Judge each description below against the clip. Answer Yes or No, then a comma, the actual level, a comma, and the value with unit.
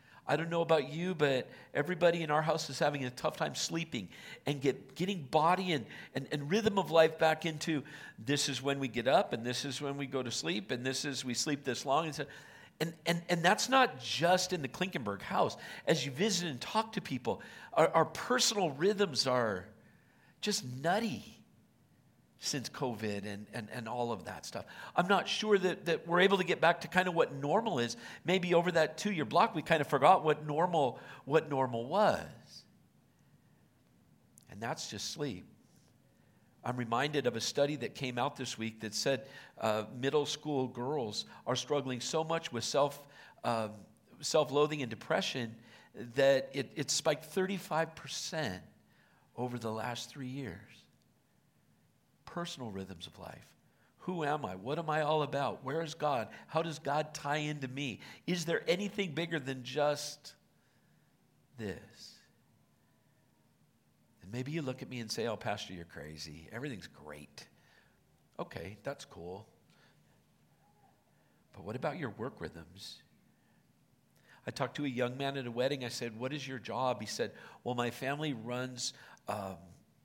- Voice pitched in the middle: Yes, medium, 145 Hz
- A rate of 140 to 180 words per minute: Yes, average, 170 wpm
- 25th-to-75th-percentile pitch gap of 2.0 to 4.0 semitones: No, average, 4.7 semitones